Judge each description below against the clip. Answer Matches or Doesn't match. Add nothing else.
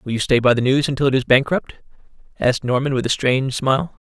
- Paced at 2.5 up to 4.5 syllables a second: Doesn't match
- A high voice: Doesn't match